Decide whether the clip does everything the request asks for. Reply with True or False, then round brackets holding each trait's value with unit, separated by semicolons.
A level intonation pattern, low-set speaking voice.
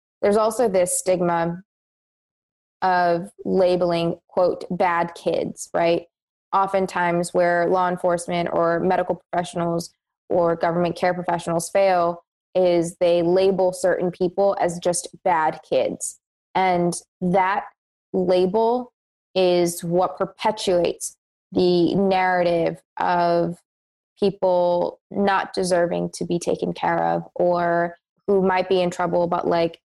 False (1.4 semitones; 180 Hz)